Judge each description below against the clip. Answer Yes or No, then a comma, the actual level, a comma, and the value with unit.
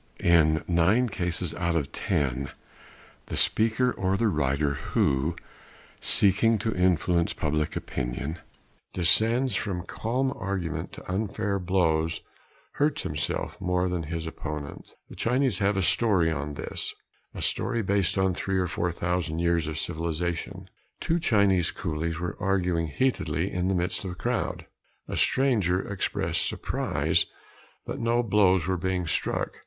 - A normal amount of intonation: Yes, average, 3.7 semitones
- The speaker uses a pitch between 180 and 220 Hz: No, very low, 90 Hz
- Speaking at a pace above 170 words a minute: No, average, 140 wpm